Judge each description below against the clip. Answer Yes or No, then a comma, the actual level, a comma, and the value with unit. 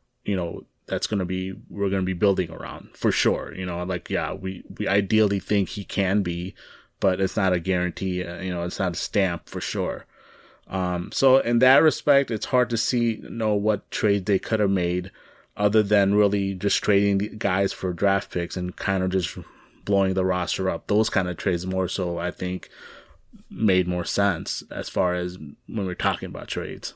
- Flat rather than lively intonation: Yes, narrow, 2.3 semitones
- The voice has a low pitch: Yes, very low, 95 Hz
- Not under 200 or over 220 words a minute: Yes, fast, 205 wpm